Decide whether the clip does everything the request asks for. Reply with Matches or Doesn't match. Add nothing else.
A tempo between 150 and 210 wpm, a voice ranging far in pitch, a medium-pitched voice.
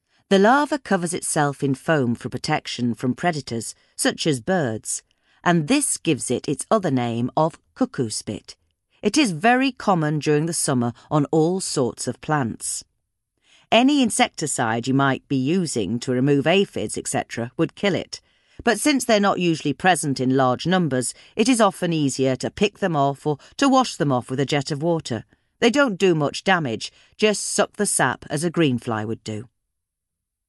Matches